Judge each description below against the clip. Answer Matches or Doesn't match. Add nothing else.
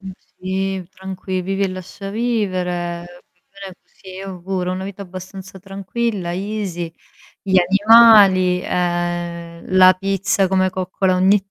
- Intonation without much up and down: Matches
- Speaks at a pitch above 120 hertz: Matches